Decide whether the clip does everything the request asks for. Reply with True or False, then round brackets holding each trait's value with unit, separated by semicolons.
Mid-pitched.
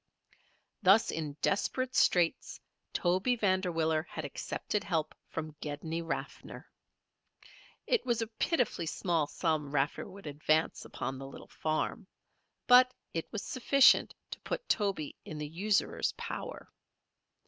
True (170 Hz)